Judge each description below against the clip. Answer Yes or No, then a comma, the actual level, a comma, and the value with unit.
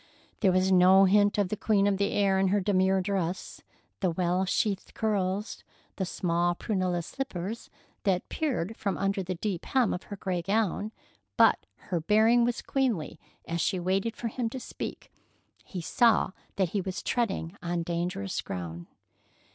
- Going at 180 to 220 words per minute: No, average, 165 wpm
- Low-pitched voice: No, high, 190 Hz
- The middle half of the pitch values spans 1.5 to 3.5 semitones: Yes, average, 2.9 semitones